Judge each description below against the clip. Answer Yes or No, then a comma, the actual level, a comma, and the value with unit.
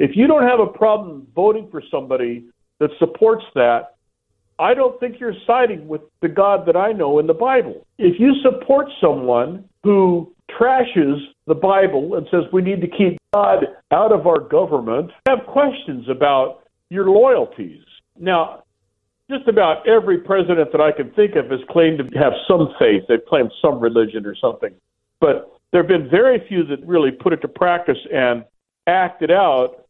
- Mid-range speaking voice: Yes, medium, 180 Hz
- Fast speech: No, average, 175 wpm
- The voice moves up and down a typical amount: No, wide, 8.7 semitones